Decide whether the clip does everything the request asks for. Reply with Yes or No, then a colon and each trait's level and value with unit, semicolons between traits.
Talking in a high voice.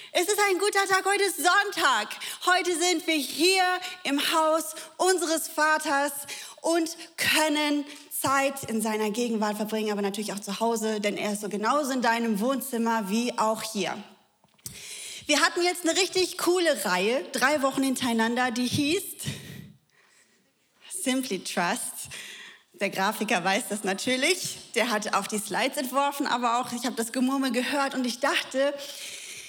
Yes: very high, 275 Hz